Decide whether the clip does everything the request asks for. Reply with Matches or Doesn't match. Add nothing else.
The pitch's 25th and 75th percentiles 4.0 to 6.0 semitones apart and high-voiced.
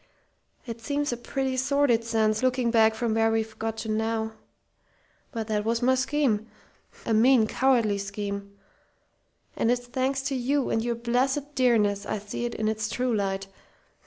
Doesn't match